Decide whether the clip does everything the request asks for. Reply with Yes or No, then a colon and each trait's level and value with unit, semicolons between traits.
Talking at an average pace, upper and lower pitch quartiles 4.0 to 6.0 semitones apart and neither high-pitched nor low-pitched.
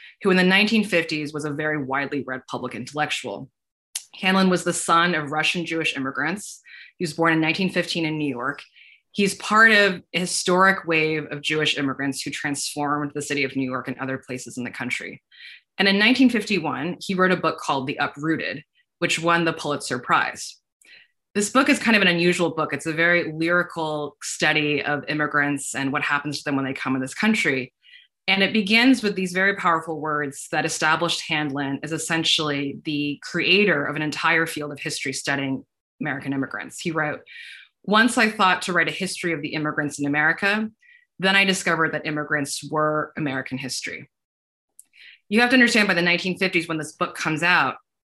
Yes: average, 185 wpm; average, 4.3 semitones; medium, 160 Hz